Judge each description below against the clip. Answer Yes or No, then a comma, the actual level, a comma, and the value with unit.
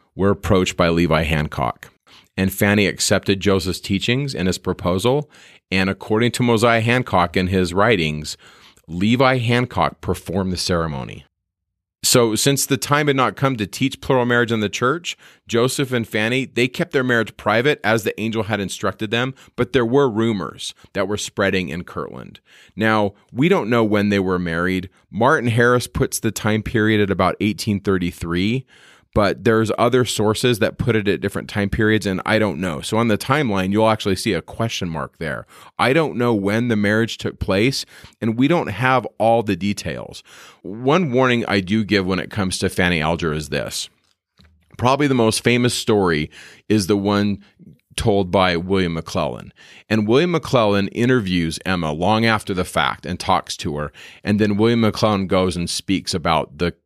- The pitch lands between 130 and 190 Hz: No, low, 105 Hz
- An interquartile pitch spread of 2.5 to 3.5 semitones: No, average, 4.1 semitones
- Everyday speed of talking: Yes, average, 180 wpm